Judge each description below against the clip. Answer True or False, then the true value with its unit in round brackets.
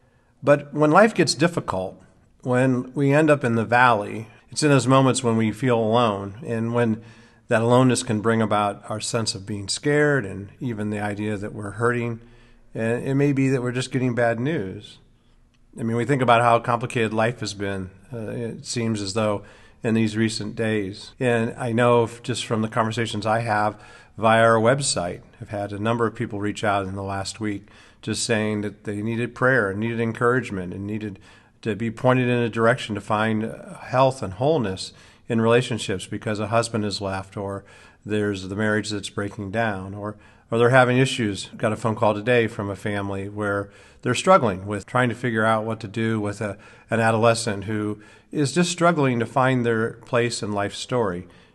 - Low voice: True (115 Hz)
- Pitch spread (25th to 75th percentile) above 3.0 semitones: False (2.6 semitones)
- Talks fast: False (195 wpm)